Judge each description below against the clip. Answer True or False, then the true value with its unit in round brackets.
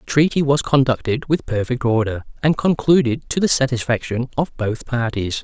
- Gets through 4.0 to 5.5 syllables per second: True (5.1 syllables/s)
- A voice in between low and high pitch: False (130 Hz)